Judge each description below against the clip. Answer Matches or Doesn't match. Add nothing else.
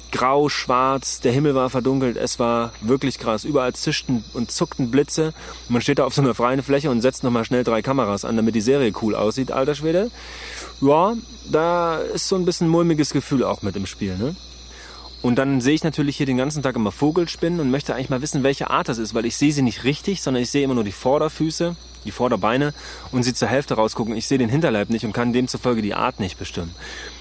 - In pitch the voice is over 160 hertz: Doesn't match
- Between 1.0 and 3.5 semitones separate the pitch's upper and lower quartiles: Doesn't match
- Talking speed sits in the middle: Doesn't match